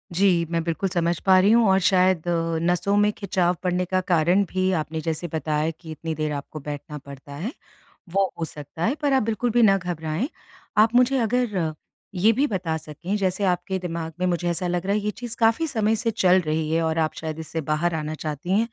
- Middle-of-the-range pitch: Yes, medium, 180 Hz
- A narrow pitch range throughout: No, average, 4.3 semitones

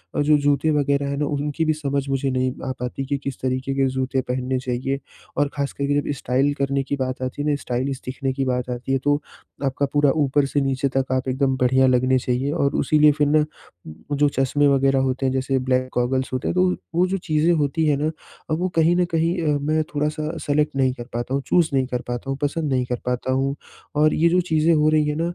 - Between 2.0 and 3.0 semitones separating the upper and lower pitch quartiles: Yes, narrow, 2.4 semitones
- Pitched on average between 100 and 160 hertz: Yes, medium, 140 Hz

